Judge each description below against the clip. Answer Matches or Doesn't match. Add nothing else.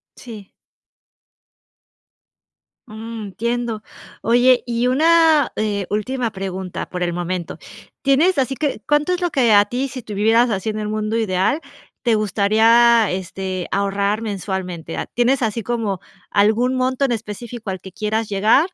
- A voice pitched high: Matches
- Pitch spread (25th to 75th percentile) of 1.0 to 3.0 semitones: Doesn't match